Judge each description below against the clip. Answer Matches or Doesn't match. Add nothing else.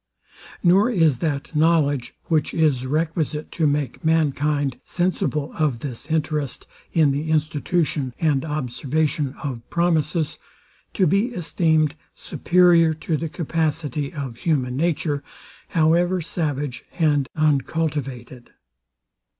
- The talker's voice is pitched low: Doesn't match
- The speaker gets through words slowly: Matches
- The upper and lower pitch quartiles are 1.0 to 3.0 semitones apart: Matches